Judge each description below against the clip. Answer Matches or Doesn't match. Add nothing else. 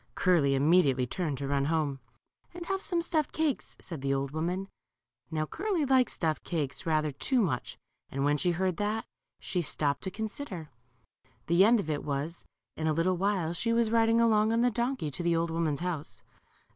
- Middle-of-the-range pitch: Matches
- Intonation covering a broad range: Matches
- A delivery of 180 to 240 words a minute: Matches